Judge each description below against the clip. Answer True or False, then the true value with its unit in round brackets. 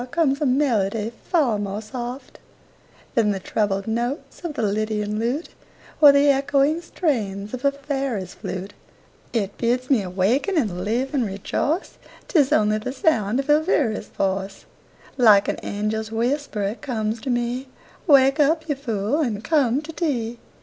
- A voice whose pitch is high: True (240 Hz)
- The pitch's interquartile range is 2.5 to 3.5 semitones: False (5.1 semitones)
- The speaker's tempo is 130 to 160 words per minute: True (155 wpm)